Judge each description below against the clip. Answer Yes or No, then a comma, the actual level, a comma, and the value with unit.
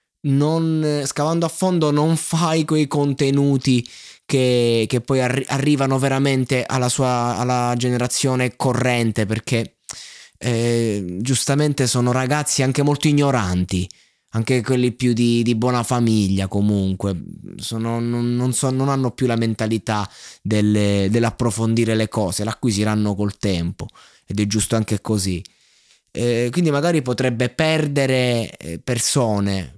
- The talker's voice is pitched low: Yes, low, 125 Hz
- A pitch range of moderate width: Yes, average, 3.6 semitones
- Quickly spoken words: No, average, 125 wpm